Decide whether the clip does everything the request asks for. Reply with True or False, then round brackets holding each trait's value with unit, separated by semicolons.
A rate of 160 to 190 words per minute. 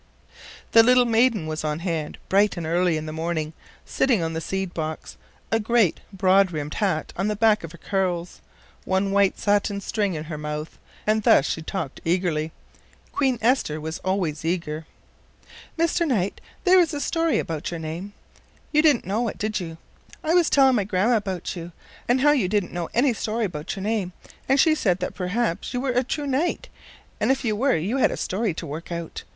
False (200 wpm)